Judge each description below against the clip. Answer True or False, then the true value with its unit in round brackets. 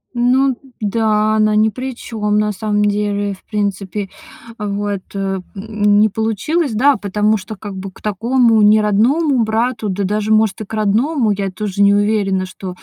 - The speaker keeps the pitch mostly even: True (1.6 semitones)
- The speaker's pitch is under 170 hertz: False (210 Hz)